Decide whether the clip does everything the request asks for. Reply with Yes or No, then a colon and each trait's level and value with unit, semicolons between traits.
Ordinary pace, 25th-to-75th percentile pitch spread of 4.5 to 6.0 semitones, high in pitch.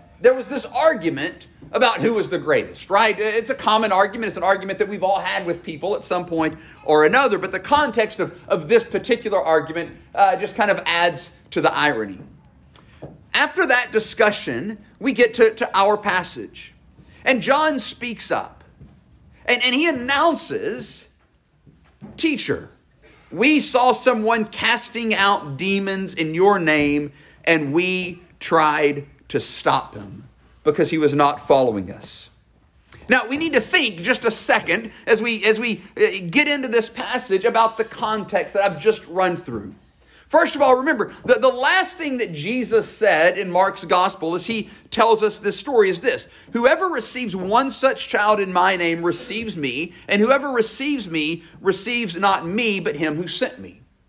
Yes: average, 170 wpm; wide, 5.5 semitones; high, 210 Hz